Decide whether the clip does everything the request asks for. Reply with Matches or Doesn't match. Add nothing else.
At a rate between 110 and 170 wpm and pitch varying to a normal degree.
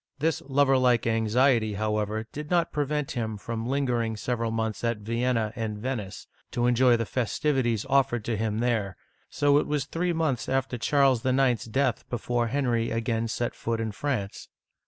Matches